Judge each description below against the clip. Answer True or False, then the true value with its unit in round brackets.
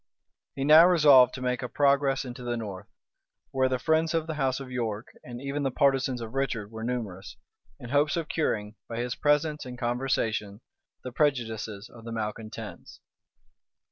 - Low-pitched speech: True (125 Hz)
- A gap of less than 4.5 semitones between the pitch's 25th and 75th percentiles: True (3.6 semitones)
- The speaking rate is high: False (170 wpm)